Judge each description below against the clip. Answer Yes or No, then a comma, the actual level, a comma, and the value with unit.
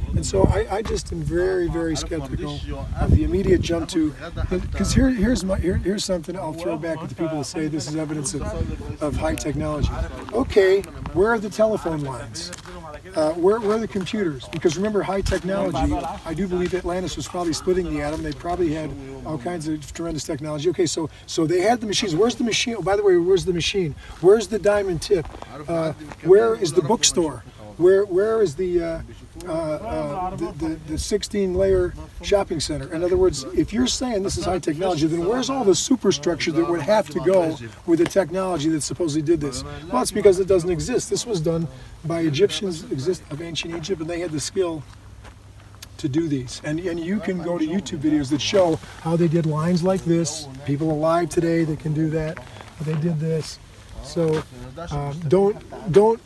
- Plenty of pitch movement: No, average, 3.9 semitones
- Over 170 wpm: Yes, average, 200 wpm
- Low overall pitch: No, medium, 170 Hz